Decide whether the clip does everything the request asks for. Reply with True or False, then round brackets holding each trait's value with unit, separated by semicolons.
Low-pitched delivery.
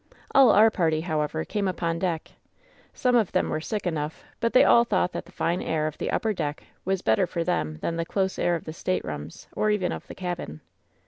False (175 Hz)